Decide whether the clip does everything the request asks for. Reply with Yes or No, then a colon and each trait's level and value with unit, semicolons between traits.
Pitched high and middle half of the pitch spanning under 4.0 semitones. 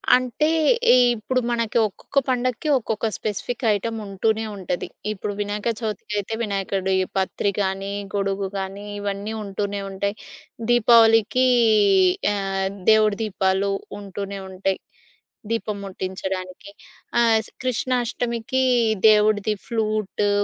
Yes: high, 205 Hz; narrow, 2.6 semitones